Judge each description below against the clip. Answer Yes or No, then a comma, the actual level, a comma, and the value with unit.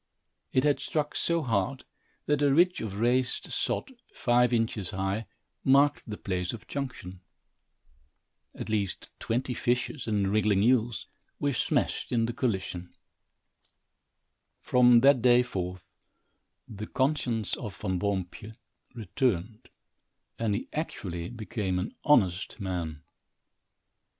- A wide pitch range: No, average, 4.8 semitones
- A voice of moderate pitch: No, low, 115 Hz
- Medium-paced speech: No, slow, 120 wpm